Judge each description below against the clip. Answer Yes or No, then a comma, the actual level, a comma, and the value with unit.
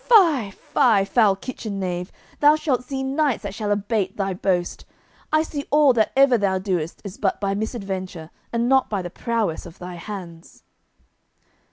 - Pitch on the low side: No, high, 205 Hz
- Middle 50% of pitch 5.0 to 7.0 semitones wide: Yes, wide, 5.6 semitones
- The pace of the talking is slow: No, average, 165 wpm